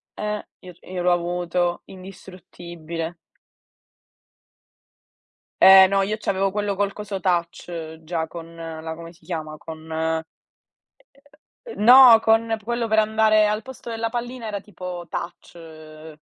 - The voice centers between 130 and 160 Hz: No, medium, 180 Hz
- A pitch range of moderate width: Yes, average, 4.1 semitones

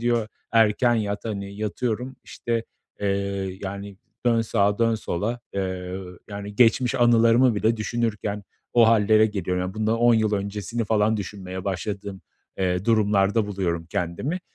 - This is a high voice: No, low, 105 Hz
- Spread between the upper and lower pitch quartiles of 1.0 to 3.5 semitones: Yes, narrow, 2.6 semitones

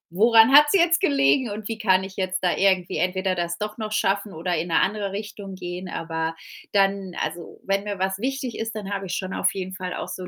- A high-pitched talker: Yes, high, 195 Hz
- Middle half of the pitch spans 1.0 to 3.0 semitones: Yes, average, 2.7 semitones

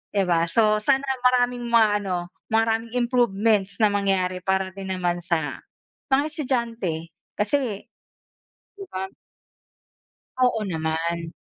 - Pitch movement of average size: Yes, average, 4.6 semitones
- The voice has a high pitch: Yes, high, 205 Hz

